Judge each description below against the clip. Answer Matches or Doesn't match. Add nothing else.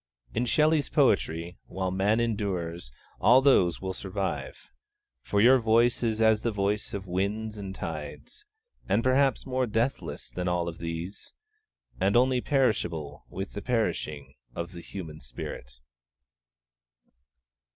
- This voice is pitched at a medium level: Doesn't match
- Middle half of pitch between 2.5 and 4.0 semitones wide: Doesn't match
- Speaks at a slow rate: Matches